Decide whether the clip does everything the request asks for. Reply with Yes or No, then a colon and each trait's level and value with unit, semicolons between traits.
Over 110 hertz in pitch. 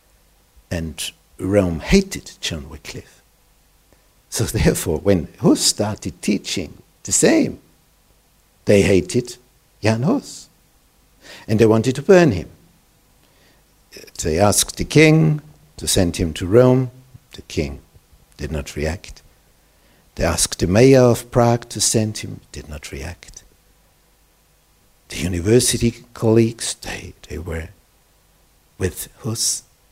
No: low, 105 Hz